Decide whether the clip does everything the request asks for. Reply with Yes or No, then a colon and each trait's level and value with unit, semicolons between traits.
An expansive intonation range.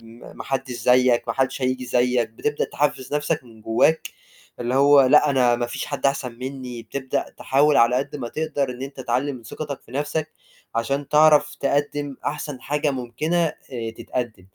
No: average, 3.0 semitones